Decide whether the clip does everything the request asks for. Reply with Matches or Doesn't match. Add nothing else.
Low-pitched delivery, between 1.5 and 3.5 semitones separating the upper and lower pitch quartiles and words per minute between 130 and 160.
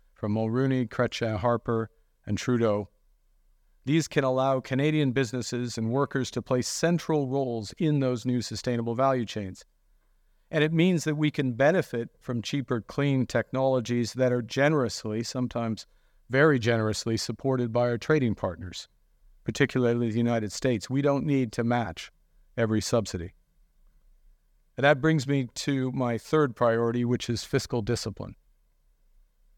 Matches